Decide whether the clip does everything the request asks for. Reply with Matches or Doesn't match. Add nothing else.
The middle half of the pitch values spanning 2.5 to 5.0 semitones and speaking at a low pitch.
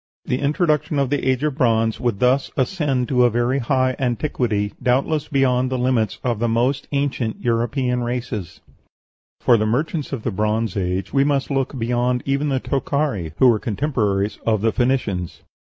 Matches